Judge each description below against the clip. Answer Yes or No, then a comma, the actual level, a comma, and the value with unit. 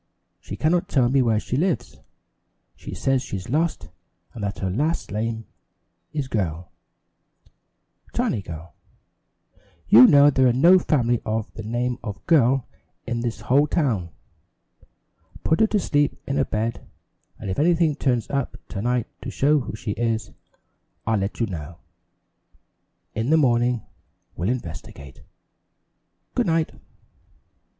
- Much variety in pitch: No, average, 5.0 semitones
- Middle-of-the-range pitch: No, low, 120 Hz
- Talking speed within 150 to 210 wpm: No, average, 140 wpm